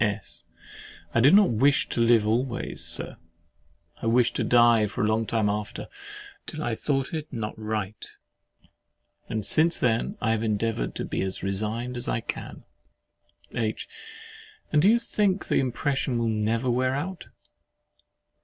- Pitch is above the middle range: No, low, 115 Hz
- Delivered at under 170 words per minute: Yes, average, 155 wpm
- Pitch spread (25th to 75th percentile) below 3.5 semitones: No, average, 4.0 semitones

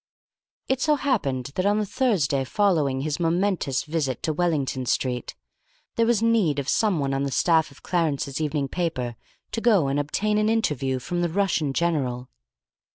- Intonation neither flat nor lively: No, wide, 6.8 semitones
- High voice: No, medium, 160 Hz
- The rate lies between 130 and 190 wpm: Yes, average, 165 wpm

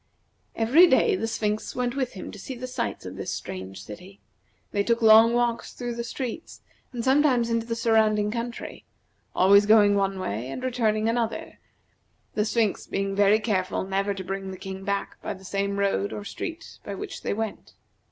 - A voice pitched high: Yes, high, 215 Hz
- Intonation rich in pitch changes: No, average, 3.1 semitones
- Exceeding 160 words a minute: Yes, average, 185 wpm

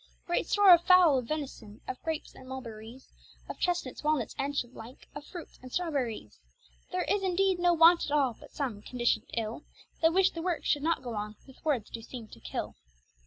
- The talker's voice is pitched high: Yes, very high, 280 Hz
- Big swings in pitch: Yes, wide, 6.2 semitones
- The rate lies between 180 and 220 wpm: Yes, fast, 205 wpm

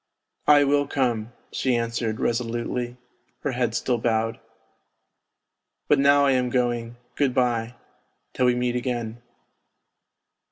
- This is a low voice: Yes, low, 120 Hz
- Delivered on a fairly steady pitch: Yes, narrow, 1.7 semitones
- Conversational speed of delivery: No, slow, 130 wpm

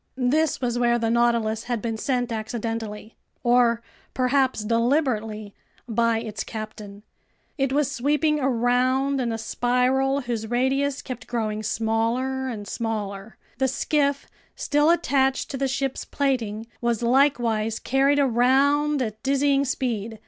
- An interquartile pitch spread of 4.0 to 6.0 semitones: No, average, 3.2 semitones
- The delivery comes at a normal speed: No, slow, 125 wpm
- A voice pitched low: No, high, 245 Hz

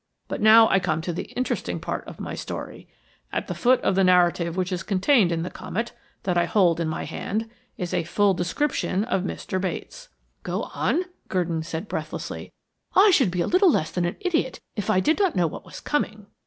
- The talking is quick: Yes, fast, 210 wpm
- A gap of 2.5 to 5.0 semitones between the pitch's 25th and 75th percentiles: No, wide, 5.4 semitones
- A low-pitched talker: No, medium, 185 Hz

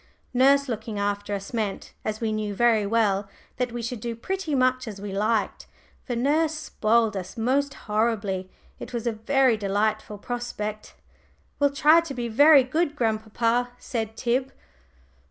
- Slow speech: No, average, 155 wpm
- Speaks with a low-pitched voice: No, high, 230 Hz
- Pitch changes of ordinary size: Yes, average, 3.3 semitones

